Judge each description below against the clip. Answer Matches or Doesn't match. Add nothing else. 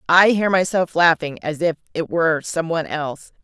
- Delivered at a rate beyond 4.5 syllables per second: Matches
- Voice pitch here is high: Doesn't match